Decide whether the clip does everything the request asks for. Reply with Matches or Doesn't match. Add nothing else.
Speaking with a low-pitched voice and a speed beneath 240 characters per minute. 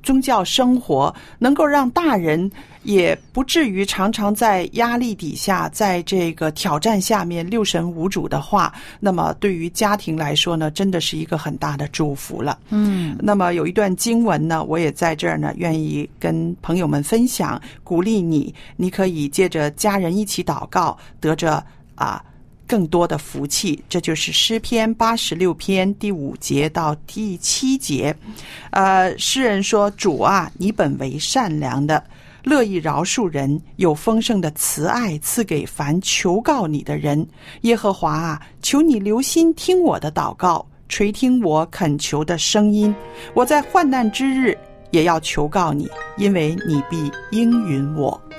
Doesn't match